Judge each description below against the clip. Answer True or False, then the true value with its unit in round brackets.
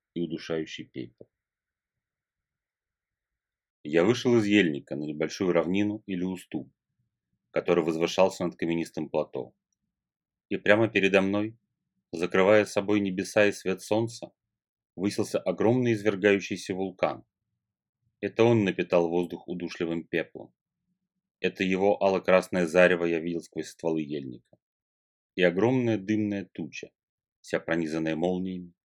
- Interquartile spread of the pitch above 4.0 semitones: False (3.6 semitones)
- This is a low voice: True (95 Hz)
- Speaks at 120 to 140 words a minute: False (110 wpm)